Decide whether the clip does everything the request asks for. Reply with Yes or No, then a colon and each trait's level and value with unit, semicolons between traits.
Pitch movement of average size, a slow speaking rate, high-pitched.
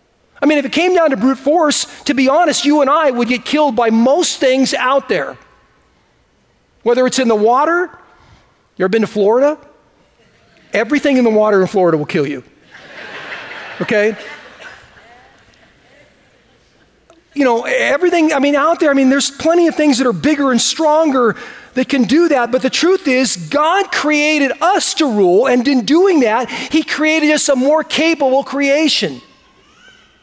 No: average, 3.6 semitones; average, 170 wpm; very high, 280 Hz